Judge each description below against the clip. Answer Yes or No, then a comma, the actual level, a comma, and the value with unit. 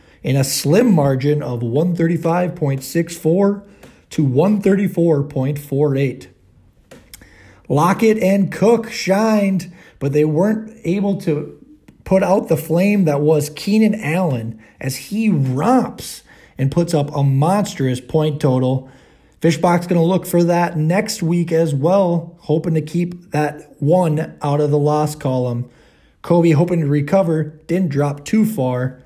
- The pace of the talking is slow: Yes, slow, 130 wpm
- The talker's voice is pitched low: No, medium, 160 Hz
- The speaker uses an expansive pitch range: No, average, 4.4 semitones